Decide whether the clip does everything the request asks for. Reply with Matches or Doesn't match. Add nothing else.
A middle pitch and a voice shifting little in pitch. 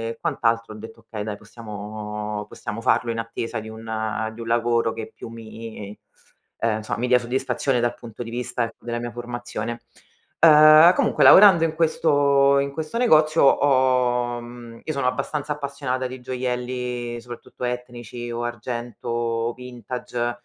Doesn't match